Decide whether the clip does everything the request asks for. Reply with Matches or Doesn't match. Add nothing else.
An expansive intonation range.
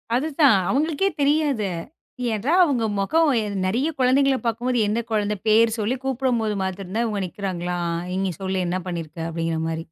Matches